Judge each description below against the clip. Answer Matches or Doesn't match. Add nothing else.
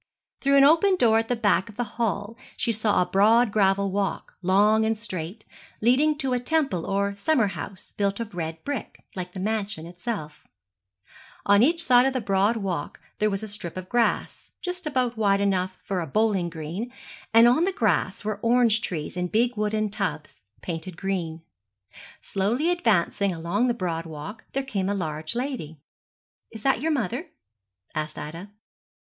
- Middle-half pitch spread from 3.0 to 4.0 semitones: Doesn't match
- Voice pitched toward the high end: Matches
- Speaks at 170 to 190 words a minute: Matches